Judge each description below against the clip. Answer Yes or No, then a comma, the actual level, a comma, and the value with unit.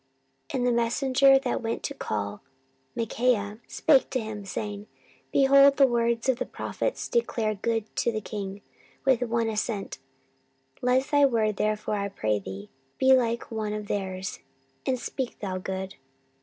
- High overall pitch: Yes, high, 225 Hz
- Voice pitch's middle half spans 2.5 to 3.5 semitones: No, average, 3.9 semitones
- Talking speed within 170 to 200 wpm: No, average, 155 wpm